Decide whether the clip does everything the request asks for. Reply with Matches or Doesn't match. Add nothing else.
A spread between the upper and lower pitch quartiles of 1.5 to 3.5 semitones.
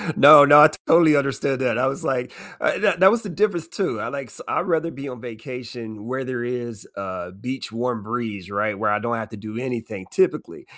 Doesn't match